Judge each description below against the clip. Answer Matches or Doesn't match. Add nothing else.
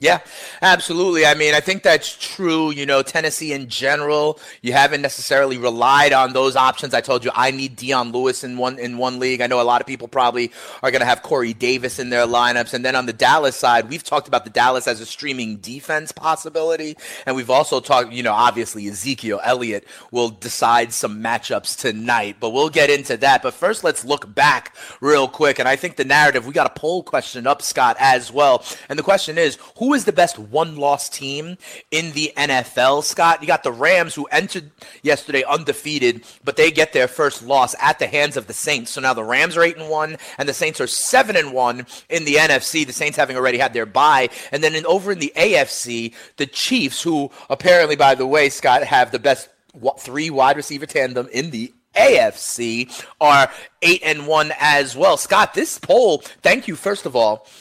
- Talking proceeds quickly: Matches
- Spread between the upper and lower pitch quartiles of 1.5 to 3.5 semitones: Doesn't match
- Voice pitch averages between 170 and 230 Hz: Doesn't match